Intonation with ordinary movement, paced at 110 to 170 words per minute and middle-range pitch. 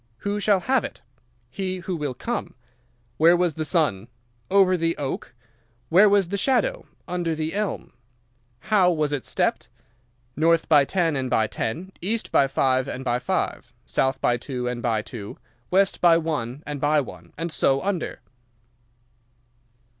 No: wide, 5.9 semitones; average, 160 wpm; medium, 160 Hz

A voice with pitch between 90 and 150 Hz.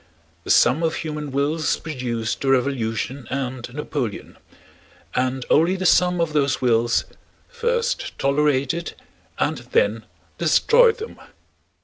Yes: medium, 140 Hz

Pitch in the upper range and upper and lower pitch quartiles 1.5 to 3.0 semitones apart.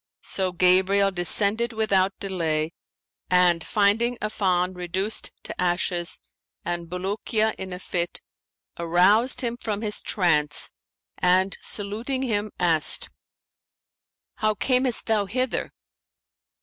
No: high, 195 Hz; average, 3.4 semitones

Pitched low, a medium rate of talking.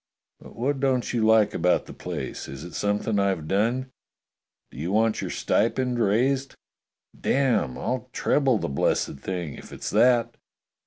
Yes: low, 110 Hz; average, 155 wpm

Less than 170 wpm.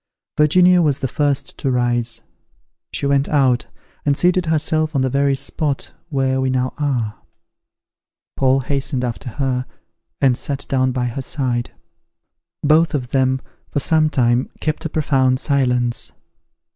Yes: average, 145 wpm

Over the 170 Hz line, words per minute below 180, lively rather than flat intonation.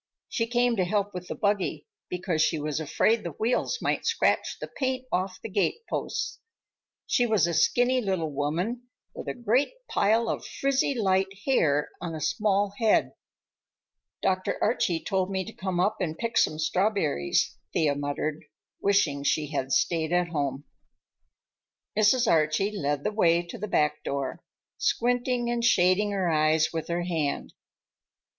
Yes: medium, 185 Hz; average, 155 wpm; wide, 5.9 semitones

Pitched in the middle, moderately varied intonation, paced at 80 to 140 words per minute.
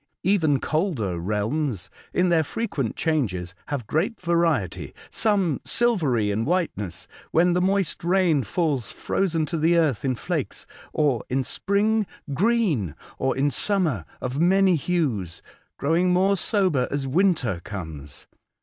No: medium, 155 Hz; wide, 7.2 semitones; slow, 135 wpm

